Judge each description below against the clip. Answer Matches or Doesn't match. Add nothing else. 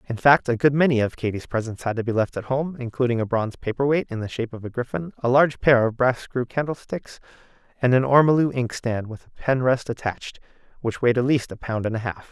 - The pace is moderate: Doesn't match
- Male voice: Matches